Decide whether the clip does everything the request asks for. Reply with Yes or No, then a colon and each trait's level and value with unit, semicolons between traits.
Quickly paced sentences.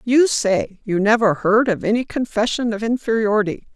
No: average, 160 wpm